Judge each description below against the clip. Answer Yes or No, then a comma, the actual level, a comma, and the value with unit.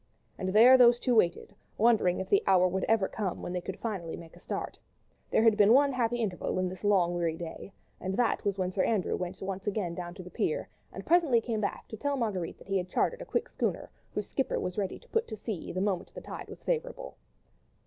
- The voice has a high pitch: Yes, high, 200 Hz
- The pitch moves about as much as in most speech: Yes, average, 4.4 semitones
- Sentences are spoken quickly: Yes, fast, 240 wpm